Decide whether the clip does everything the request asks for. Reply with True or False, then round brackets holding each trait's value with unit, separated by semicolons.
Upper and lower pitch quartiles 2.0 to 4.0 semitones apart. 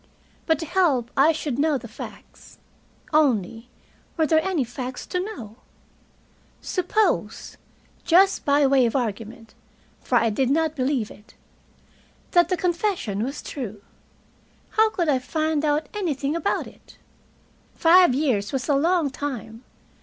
False (5.0 semitones)